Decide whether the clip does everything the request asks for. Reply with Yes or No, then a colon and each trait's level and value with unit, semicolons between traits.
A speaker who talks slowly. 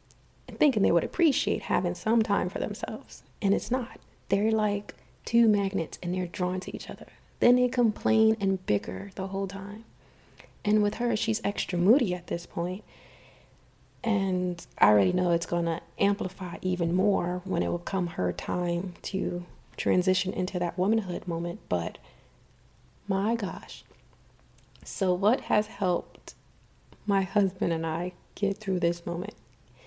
No: average, 155 wpm